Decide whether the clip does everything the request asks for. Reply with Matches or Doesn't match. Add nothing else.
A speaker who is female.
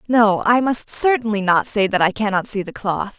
Matches